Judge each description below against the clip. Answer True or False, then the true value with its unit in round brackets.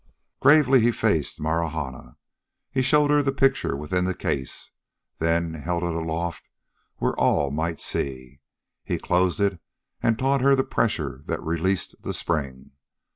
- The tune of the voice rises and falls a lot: True (7.8 semitones)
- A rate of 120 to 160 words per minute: True (145 wpm)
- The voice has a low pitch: True (85 Hz)